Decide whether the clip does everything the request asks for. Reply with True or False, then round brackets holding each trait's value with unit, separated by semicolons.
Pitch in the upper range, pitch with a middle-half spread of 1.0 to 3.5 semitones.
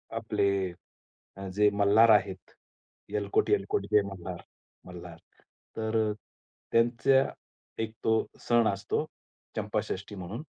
False (105 Hz; 2.6 semitones)